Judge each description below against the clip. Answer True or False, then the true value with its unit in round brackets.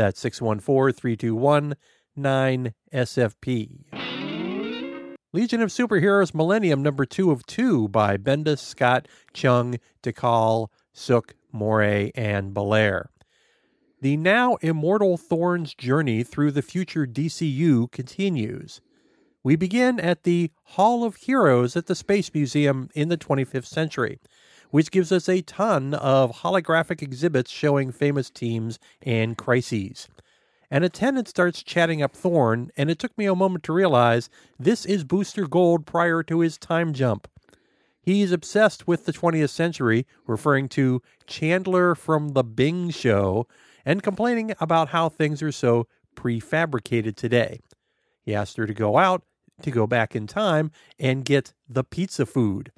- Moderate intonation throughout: False (6.0 semitones)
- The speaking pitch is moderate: True (145 Hz)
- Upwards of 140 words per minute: False (135 wpm)